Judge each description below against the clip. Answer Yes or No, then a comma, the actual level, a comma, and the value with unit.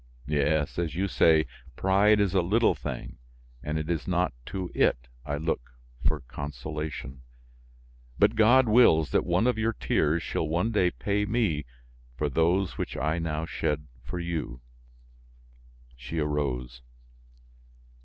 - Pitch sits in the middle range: No, very low, 80 Hz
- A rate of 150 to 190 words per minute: No, average, 140 wpm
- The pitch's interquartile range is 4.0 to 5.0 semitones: Yes, average, 4.6 semitones